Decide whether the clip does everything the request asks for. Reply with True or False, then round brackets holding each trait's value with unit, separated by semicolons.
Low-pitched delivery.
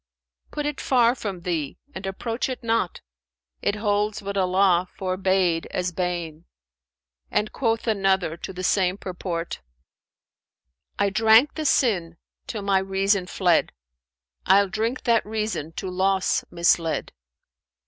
False (190 Hz)